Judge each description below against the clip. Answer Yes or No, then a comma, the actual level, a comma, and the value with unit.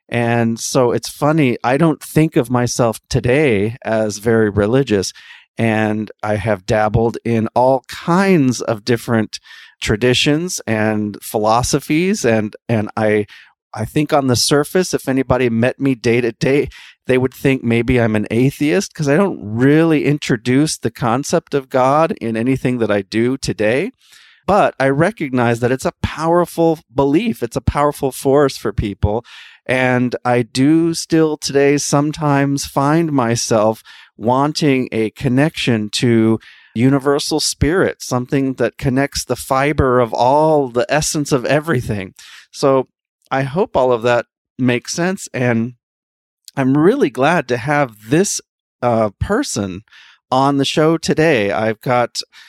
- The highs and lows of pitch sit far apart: No, average, 4.1 semitones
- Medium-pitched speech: No, low, 130 Hz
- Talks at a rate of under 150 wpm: Yes, average, 140 wpm